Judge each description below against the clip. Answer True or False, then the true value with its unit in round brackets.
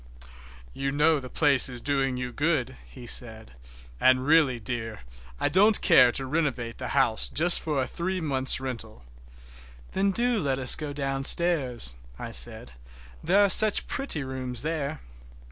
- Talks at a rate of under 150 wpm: False (155 wpm)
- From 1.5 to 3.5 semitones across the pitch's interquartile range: False (4.3 semitones)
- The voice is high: False (135 Hz)